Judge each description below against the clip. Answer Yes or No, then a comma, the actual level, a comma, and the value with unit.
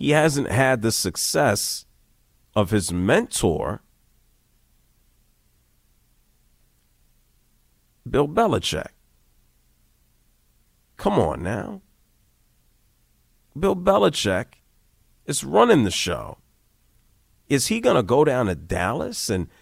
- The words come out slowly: Yes, slow, 85 wpm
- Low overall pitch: Yes, low, 105 Hz